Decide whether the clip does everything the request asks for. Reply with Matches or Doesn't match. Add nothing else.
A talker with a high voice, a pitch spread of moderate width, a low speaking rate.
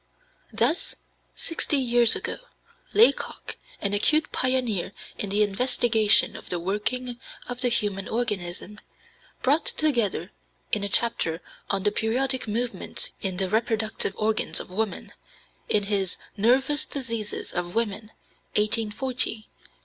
Matches